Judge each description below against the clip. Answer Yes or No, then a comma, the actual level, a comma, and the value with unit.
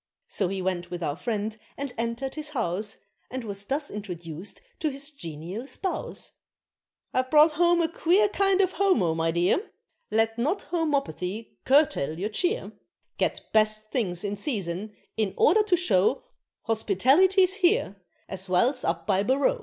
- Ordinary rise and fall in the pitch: No, wide, 8.6 semitones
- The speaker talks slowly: No, average, 155 wpm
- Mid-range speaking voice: No, high, 225 Hz